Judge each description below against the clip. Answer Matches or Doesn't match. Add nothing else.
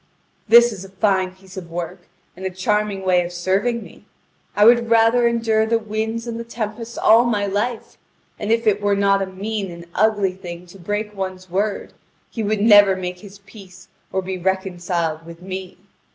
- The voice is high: Matches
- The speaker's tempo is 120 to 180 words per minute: Doesn't match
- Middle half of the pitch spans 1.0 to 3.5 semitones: Matches